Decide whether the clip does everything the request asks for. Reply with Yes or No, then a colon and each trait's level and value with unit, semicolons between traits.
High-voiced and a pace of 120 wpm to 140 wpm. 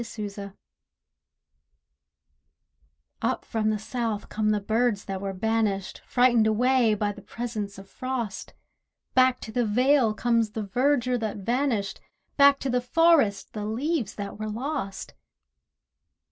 Yes: high, 225 Hz; slow, 135 wpm